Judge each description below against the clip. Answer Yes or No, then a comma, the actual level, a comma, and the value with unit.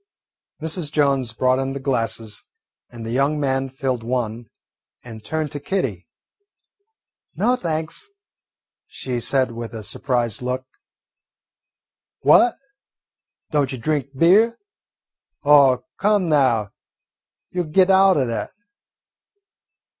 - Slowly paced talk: Yes, slow, 115 wpm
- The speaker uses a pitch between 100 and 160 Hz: Yes, low, 135 Hz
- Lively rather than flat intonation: No, average, 4.6 semitones